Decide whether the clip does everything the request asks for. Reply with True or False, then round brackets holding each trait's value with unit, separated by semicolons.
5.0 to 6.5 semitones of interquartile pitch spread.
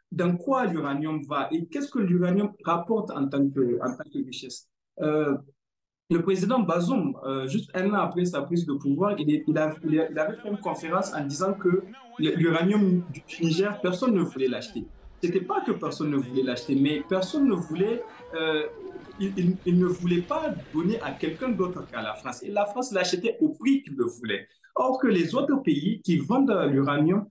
True (5.4 semitones)